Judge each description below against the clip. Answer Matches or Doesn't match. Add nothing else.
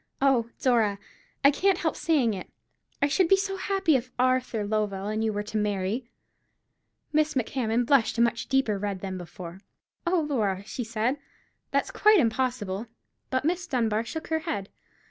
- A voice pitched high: Matches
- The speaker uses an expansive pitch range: Matches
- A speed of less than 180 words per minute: Matches